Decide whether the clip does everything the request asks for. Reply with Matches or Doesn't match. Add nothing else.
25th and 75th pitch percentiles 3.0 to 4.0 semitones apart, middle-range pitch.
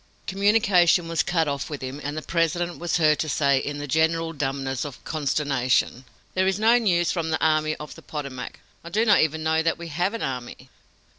Matches